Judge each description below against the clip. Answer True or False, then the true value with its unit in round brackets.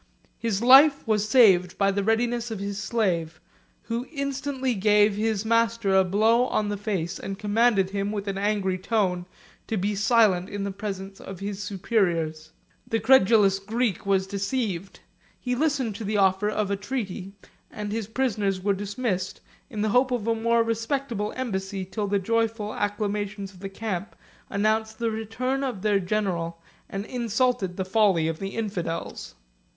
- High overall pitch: True (210 Hz)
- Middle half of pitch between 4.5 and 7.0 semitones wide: False (2.8 semitones)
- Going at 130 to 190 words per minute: True (165 wpm)